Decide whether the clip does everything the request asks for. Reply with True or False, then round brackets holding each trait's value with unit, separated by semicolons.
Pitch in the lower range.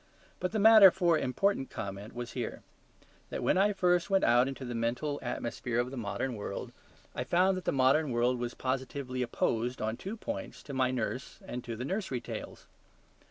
True (130 Hz)